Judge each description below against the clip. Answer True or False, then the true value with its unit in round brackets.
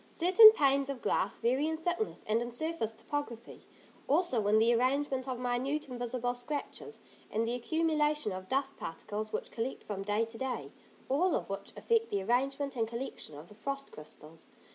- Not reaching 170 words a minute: False (175 wpm)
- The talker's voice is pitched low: False (255 Hz)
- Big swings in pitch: False (4.3 semitones)